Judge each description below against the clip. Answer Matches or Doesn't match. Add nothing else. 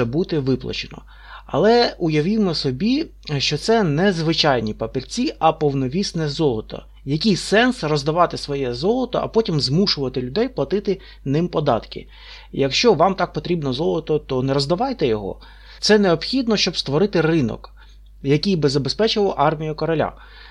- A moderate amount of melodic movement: Doesn't match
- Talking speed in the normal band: Matches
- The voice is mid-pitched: Matches